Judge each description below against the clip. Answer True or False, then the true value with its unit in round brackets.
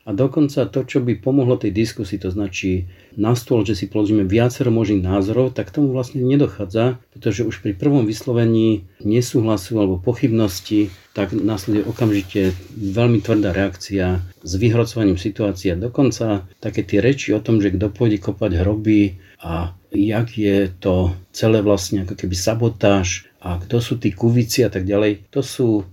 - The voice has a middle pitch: False (105 Hz)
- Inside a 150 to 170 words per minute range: True (160 wpm)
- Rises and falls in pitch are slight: False (3.2 semitones)